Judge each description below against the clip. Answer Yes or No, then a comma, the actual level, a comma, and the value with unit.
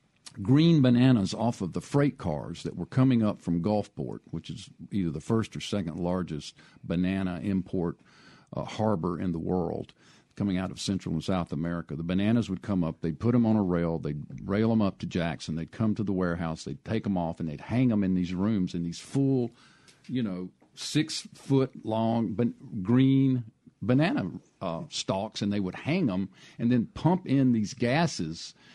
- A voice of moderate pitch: No, low, 100 Hz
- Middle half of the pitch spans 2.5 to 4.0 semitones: No, average, 5.3 semitones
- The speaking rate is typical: Yes, average, 190 wpm